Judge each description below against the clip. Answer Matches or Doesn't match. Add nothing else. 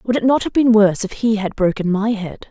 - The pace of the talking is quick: Matches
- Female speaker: Matches